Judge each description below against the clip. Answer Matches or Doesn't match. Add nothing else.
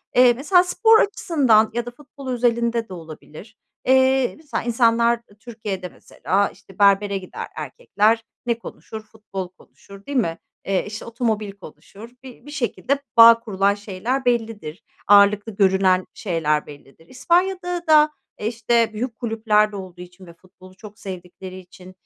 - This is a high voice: Matches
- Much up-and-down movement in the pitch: Doesn't match